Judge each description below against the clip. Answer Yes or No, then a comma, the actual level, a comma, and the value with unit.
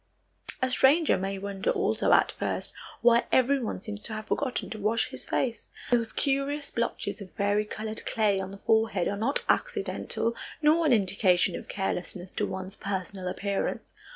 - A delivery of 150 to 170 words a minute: Yes, average, 160 wpm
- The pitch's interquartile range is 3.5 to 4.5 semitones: Yes, average, 3.9 semitones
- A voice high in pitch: Yes, high, 215 Hz